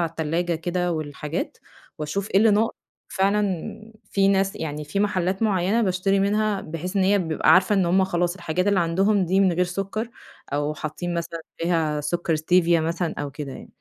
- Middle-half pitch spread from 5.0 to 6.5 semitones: No, average, 3.1 semitones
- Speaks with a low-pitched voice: No, medium, 180 Hz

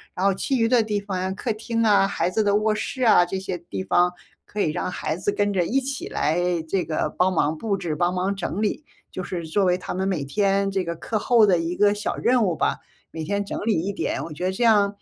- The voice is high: Yes, high, 195 Hz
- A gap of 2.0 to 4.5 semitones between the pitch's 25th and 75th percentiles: Yes, average, 3.1 semitones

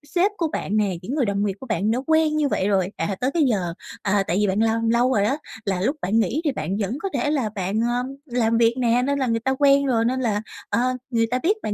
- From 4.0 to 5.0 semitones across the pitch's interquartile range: Yes, average, 4.5 semitones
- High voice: Yes, high, 230 Hz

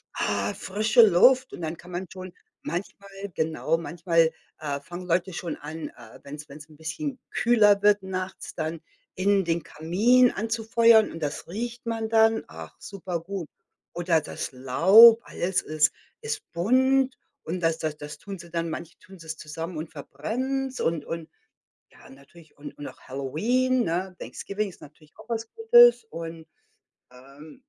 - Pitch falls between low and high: Yes, medium, 175 Hz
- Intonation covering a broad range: Yes, wide, 5.9 semitones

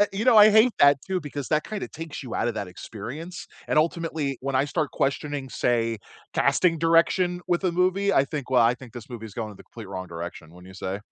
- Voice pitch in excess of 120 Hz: Yes, medium, 140 Hz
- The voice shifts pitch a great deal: Yes, wide, 7.0 semitones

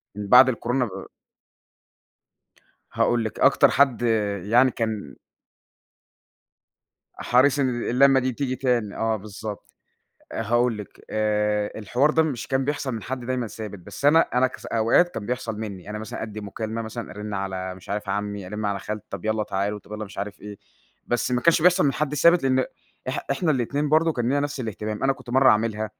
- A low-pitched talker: Yes, low, 115 Hz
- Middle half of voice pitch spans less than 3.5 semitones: No, average, 3.8 semitones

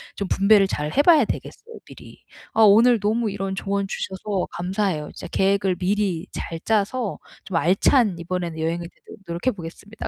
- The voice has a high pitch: Yes, high, 195 Hz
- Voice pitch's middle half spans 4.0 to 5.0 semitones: No, average, 3.2 semitones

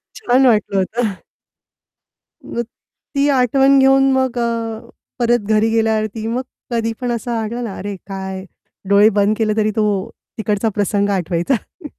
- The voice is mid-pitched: No, high, 225 Hz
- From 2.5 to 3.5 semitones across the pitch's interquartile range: Yes, average, 2.8 semitones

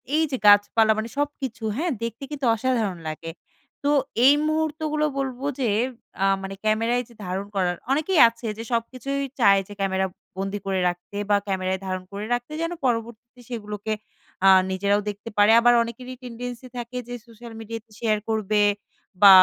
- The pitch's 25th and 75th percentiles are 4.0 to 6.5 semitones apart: No, average, 3.6 semitones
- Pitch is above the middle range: Yes, high, 230 Hz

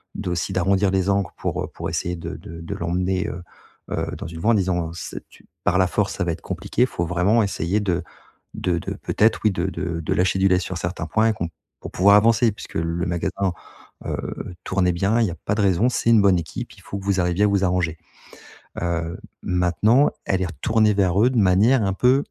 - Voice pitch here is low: Yes, very low, 95 Hz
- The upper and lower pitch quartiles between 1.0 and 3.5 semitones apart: Yes, average, 2.8 semitones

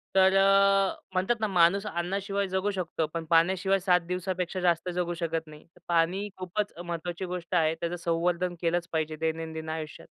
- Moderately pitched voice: Yes, medium, 175 Hz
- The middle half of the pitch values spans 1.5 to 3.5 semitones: Yes, narrow, 2.4 semitones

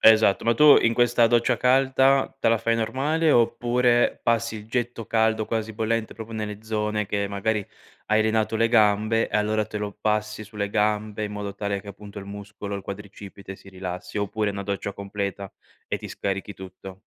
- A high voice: No, low, 105 Hz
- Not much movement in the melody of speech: Yes, narrow, 2.1 semitones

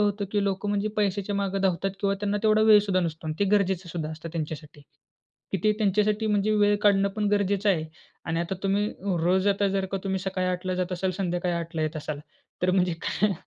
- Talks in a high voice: Yes, high, 195 Hz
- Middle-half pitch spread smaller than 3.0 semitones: Yes, narrow, 2.5 semitones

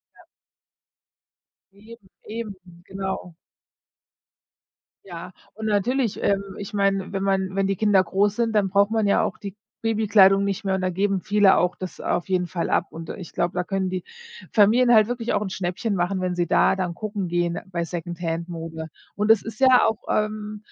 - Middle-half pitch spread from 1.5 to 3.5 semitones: Yes, average, 2.7 semitones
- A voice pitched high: Yes, high, 195 Hz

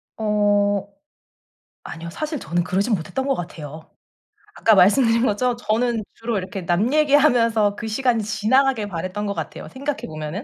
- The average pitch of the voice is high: Yes, high, 215 Hz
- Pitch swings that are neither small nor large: Yes, average, 4.4 semitones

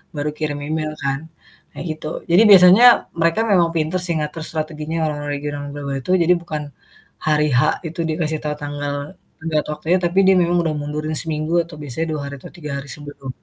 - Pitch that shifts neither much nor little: No, narrow, 2.3 semitones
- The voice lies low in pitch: No, medium, 155 Hz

